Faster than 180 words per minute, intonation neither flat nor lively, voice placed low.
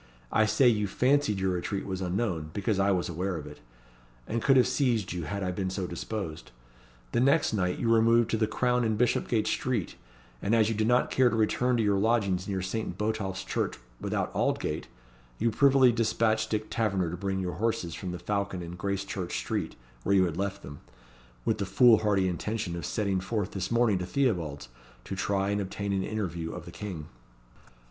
Yes: average, 200 wpm; average, 3.5 semitones; low, 100 Hz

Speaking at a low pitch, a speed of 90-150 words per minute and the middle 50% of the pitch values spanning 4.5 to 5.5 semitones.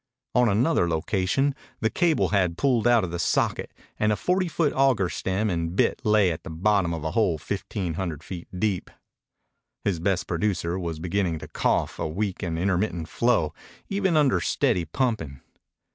No: very low, 95 Hz; average, 175 wpm; average, 4.8 semitones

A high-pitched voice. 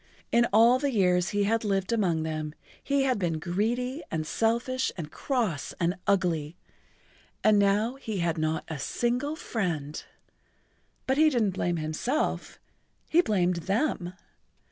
Yes: high, 200 Hz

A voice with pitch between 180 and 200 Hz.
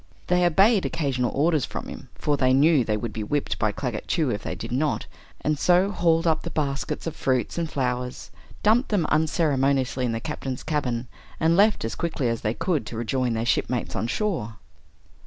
No: medium, 140 Hz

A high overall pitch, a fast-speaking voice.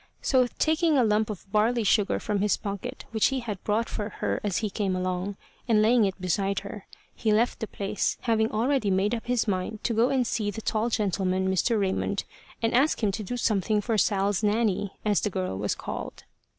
Yes: high, 210 Hz; fast, 210 wpm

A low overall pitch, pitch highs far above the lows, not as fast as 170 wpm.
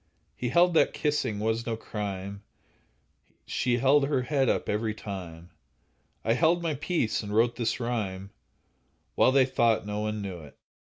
No: low, 115 Hz; average, 4.5 semitones; average, 160 wpm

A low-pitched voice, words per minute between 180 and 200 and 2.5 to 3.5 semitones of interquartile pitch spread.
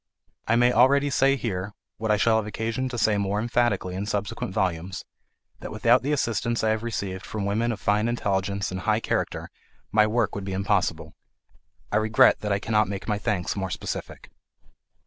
Yes: low, 105 Hz; average, 185 wpm; average, 2.8 semitones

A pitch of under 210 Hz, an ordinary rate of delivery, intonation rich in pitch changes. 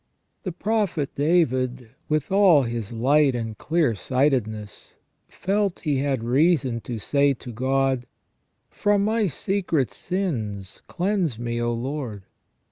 No: low, 135 Hz; slow, 125 wpm; wide, 6.5 semitones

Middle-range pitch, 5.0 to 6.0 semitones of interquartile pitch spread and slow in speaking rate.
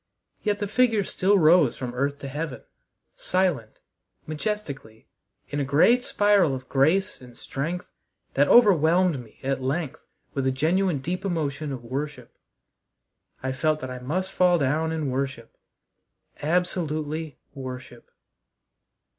Yes: medium, 155 Hz; average, 5.3 semitones; slow, 130 wpm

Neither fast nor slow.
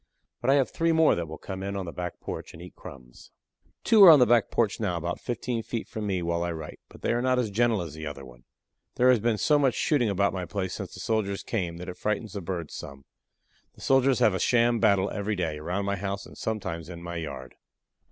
No: fast, 250 wpm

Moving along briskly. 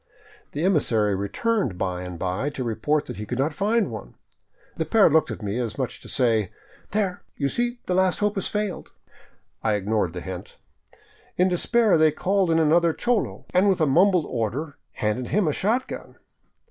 No: average, 185 wpm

